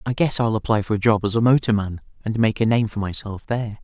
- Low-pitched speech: Yes, low, 110 Hz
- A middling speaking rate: No, fast, 265 wpm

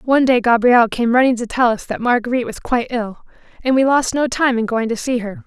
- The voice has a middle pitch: No, high, 240 Hz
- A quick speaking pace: Yes, fast, 255 wpm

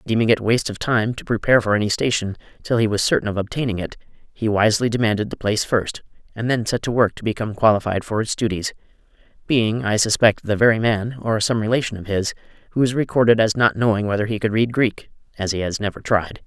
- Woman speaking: No, male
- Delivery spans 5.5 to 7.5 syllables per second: Yes, 6.4 syllables/s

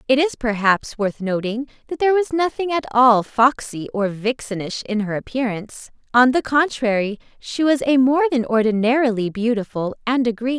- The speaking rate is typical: Yes, average, 170 wpm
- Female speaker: Yes, female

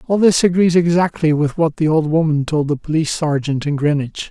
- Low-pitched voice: No, medium, 155 Hz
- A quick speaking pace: Yes, fast, 210 wpm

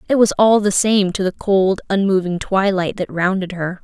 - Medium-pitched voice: No, high, 195 Hz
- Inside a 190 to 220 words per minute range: Yes, fast, 205 wpm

